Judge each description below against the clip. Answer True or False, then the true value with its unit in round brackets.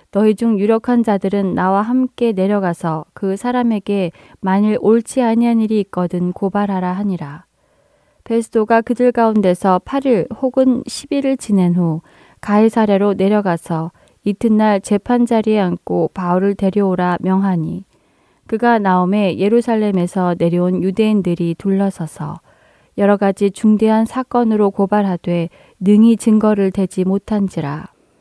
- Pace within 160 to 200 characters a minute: False (290 characters per minute)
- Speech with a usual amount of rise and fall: True (3.4 semitones)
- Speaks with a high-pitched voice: True (200 Hz)